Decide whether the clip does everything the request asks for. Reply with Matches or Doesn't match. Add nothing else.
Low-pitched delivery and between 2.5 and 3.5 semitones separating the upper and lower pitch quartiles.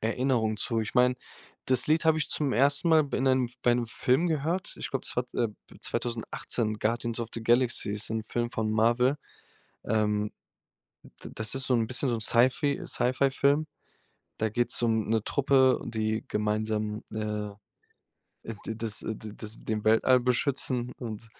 Matches